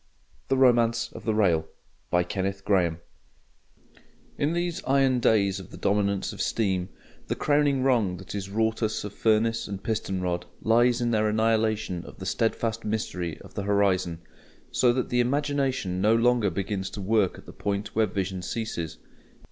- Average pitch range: Yes, average, 3.6 semitones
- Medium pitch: No, low, 105 Hz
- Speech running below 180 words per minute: Yes, average, 160 wpm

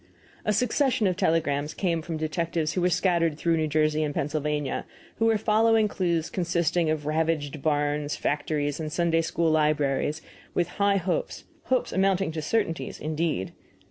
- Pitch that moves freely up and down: No, average, 3.1 semitones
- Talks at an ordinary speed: Yes, average, 160 wpm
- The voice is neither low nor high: Yes, medium, 165 Hz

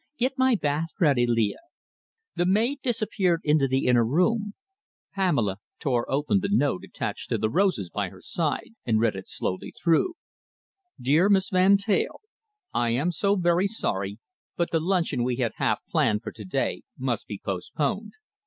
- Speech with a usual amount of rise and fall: No, wide, 8.7 semitones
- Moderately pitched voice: Yes, medium, 155 Hz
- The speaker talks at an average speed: Yes, average, 165 wpm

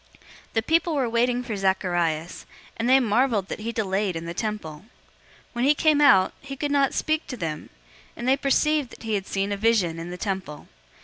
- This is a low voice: No, high, 220 Hz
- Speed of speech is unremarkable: No, fast, 210 wpm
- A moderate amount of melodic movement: No, wide, 6.0 semitones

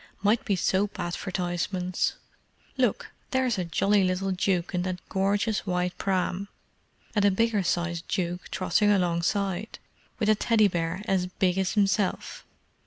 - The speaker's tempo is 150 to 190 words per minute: No, average, 140 wpm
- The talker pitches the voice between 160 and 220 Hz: Yes, high, 190 Hz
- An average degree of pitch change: No, narrow, 2.3 semitones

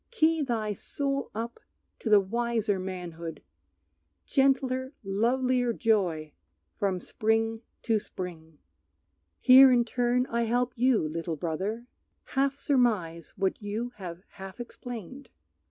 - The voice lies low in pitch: No, high, 225 Hz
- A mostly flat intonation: No, average, 4.9 semitones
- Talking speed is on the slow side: Yes, slow, 115 wpm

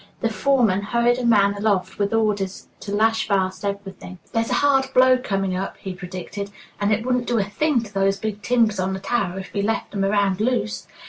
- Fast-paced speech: Yes, fast, 210 wpm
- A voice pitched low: No, high, 205 Hz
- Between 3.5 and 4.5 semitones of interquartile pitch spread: No, average, 2.9 semitones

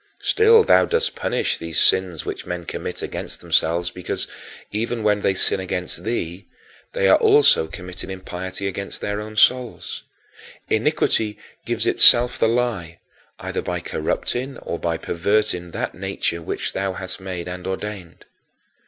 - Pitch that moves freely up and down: No, average, 4.2 semitones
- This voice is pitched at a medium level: No, very low, 95 Hz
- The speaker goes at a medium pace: Yes, average, 145 wpm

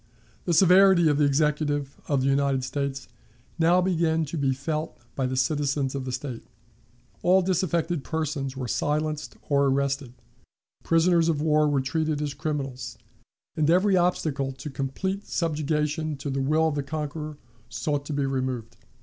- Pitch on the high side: No, medium, 150 Hz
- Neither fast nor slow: Yes, average, 160 wpm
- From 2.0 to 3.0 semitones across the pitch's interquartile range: Yes, average, 2.7 semitones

